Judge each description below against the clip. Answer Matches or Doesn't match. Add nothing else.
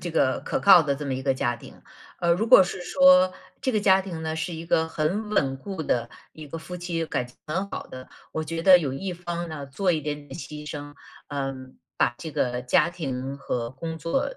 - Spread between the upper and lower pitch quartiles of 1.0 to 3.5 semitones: Doesn't match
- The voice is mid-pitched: Matches